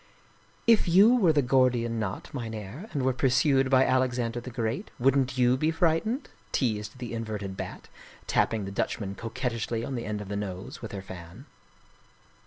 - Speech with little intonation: No, average, 3.8 semitones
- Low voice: Yes, low, 125 Hz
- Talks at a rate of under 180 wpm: No, average, 185 wpm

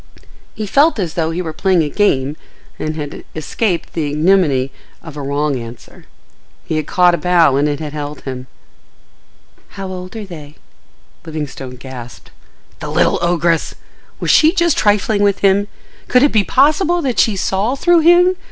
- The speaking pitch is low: No, medium, 175 Hz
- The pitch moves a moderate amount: No, wide, 5.9 semitones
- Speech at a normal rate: Yes, average, 165 wpm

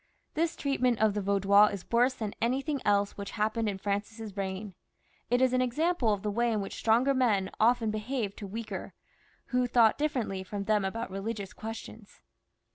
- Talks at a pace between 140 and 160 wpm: No, average, 180 wpm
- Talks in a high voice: Yes, high, 220 Hz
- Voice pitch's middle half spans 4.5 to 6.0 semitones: No, average, 3.4 semitones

